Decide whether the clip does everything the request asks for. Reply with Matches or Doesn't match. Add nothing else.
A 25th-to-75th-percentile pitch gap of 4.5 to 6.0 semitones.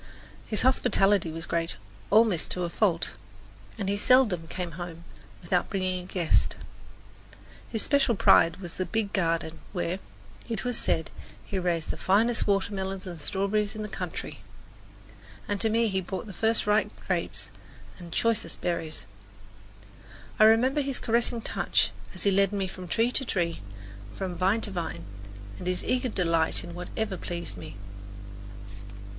Doesn't match